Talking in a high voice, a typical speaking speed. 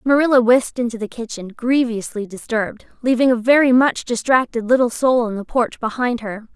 Yes: high, 240 Hz; average, 175 wpm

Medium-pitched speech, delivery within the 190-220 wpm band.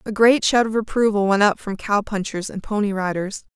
No: high, 205 Hz; fast, 205 wpm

